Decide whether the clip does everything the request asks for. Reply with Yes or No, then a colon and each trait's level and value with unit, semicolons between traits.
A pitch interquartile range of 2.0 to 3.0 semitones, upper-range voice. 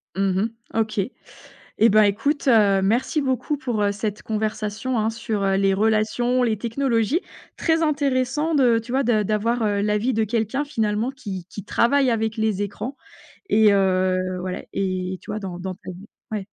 No: average, 3.6 semitones; high, 220 Hz